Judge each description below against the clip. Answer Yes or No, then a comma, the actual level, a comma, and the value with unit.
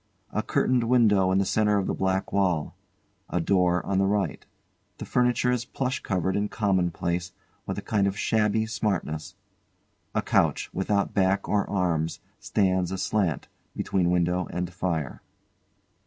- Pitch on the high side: No, very low, 95 Hz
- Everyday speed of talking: Yes, average, 150 wpm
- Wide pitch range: No, average, 2.7 semitones